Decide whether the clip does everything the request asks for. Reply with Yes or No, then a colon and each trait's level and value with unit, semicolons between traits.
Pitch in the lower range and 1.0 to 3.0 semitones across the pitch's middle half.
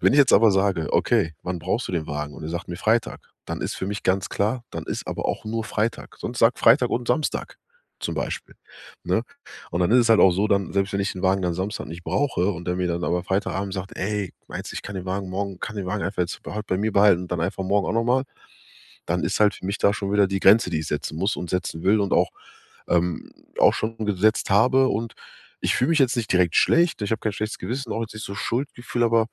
No: low, 100 Hz; average, 3.6 semitones